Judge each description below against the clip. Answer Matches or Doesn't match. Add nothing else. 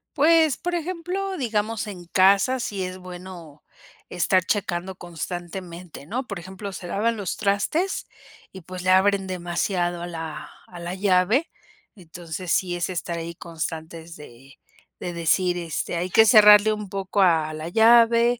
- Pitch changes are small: Doesn't match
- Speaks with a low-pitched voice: Doesn't match